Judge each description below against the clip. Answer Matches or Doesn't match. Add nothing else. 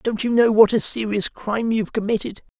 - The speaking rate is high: Matches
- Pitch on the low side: Doesn't match